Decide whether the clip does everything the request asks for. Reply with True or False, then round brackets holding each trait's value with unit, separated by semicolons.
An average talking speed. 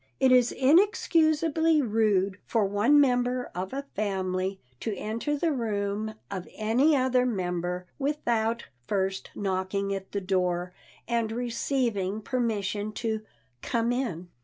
False (125 wpm)